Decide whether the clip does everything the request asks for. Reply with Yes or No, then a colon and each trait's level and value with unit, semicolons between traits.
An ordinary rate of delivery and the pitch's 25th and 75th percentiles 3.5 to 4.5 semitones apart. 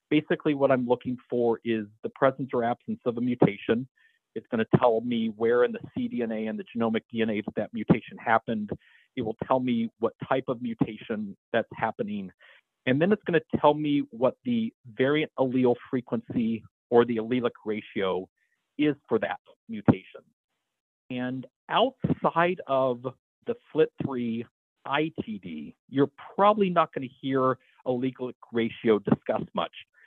No: average, 150 wpm; average, 5.3 semitones